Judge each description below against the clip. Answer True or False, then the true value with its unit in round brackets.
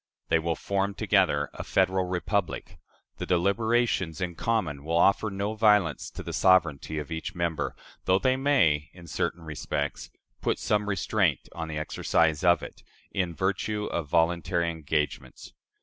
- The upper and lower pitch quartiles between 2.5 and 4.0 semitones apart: True (3.7 semitones)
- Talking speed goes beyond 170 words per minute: False (150 wpm)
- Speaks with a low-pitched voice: True (85 Hz)